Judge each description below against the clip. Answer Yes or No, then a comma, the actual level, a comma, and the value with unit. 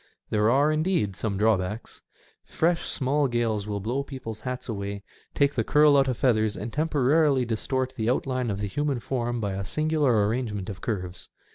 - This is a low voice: Yes, low, 120 Hz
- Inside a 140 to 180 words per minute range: Yes, average, 175 wpm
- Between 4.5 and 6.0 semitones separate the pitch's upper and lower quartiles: Yes, average, 4.9 semitones